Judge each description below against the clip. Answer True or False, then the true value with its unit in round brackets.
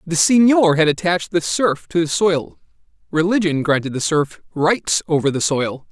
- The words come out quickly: False (175 wpm)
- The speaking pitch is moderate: True (165 Hz)